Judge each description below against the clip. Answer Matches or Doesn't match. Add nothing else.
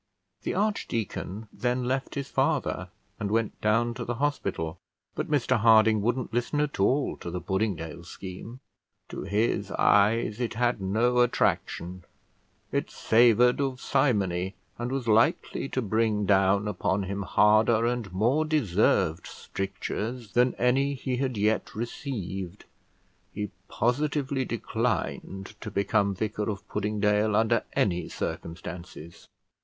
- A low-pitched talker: Matches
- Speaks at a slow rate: Matches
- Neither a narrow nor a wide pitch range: Matches